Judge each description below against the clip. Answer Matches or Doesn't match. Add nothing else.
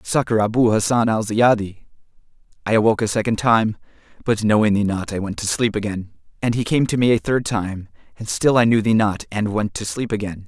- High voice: Doesn't match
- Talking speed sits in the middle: Doesn't match